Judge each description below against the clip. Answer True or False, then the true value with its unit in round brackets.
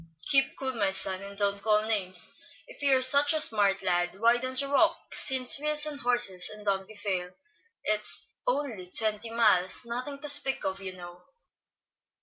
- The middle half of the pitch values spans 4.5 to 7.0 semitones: True (5.6 semitones)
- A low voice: False (220 Hz)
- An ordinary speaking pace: True (175 wpm)